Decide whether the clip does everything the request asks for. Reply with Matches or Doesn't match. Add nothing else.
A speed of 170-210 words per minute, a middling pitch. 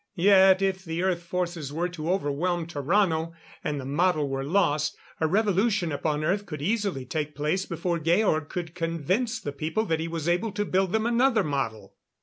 Matches